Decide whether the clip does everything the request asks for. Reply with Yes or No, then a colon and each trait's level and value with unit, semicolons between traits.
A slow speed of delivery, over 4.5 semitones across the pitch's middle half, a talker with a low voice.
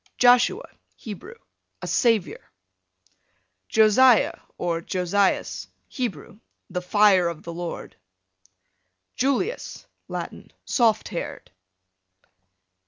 No: slow, 80 wpm; wide, 5.6 semitones; high, 210 Hz